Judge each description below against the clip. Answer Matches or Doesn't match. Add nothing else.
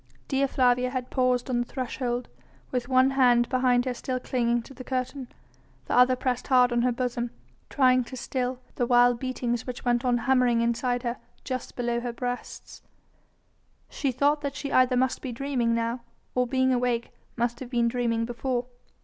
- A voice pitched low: Doesn't match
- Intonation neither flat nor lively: Doesn't match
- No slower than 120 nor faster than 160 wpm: Doesn't match